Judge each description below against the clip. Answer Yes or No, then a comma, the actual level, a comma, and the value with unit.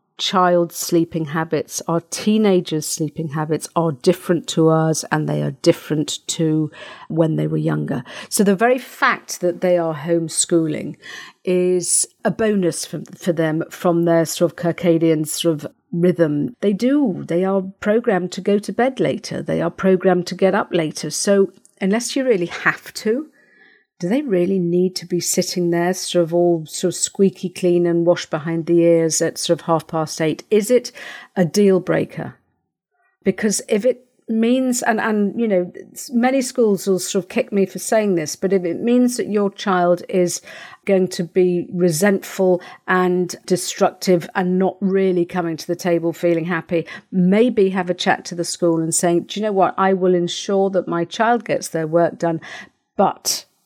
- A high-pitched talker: No, medium, 180 Hz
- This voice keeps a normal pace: Yes, average, 180 wpm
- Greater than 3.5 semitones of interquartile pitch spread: No, average, 2.9 semitones